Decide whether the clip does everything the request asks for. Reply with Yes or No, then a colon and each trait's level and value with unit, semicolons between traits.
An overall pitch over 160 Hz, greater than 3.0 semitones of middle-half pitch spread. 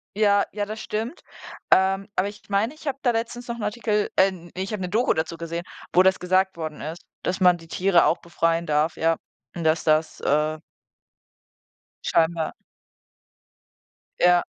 Yes: medium, 185 Hz; average, 4.0 semitones